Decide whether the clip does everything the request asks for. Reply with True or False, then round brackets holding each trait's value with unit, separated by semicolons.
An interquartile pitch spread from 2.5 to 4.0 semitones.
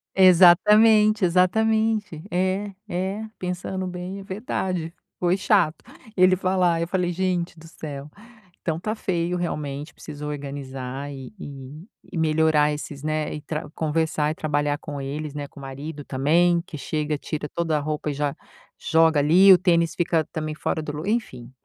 True (3.6 semitones)